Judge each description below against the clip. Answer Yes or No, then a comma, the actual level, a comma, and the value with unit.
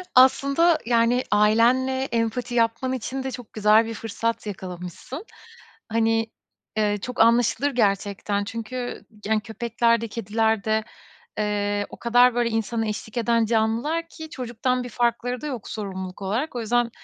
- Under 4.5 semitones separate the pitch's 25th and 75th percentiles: Yes, narrow, 2.5 semitones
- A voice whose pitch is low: No, high, 230 Hz